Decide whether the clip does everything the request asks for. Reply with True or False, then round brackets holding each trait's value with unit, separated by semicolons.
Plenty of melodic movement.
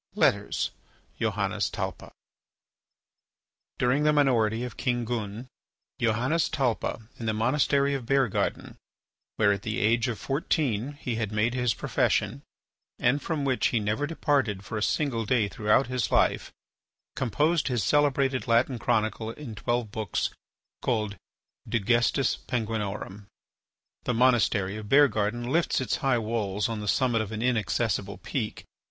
False (3.5 semitones)